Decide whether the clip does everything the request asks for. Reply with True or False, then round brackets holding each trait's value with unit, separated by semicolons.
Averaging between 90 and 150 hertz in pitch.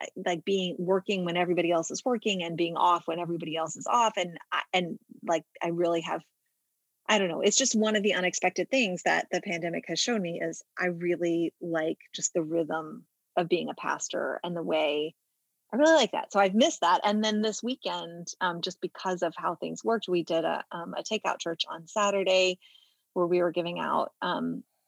False (175 Hz)